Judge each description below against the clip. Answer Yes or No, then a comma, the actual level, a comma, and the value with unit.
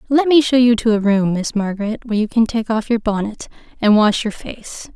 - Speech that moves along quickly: Yes, fast, 240 wpm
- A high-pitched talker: Yes, high, 225 Hz